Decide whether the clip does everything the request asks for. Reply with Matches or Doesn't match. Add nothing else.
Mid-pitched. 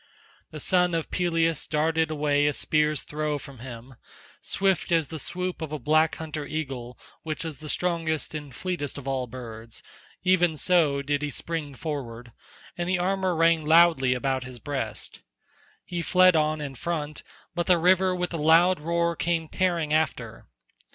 Matches